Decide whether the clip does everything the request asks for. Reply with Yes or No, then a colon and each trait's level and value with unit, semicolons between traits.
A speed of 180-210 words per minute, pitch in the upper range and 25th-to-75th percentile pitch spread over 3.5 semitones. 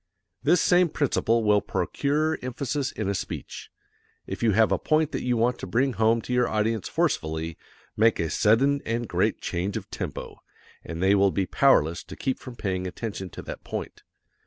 No: average, 185 wpm; low, 115 Hz; average, 5.1 semitones